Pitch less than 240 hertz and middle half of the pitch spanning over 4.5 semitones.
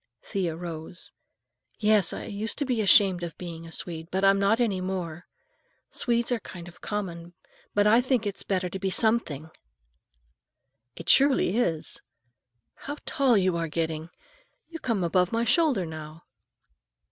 Yes: high, 190 Hz; average, 5.0 semitones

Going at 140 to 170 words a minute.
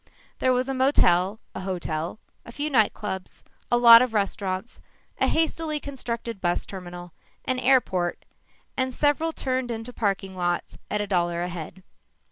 Yes: average, 155 wpm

